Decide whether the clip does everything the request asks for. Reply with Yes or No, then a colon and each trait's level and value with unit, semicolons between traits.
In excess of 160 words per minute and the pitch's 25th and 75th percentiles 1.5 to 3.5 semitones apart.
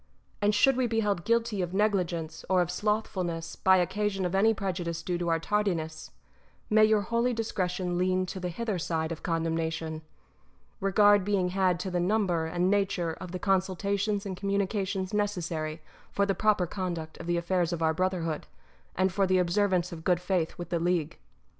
Yes: average, 185 wpm; average, 2.9 semitones